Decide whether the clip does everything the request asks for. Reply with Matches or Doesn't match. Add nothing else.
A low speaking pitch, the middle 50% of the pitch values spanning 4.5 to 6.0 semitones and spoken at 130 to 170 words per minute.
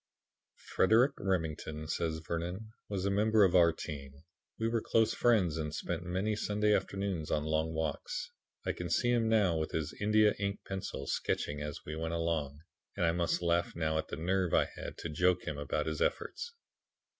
Doesn't match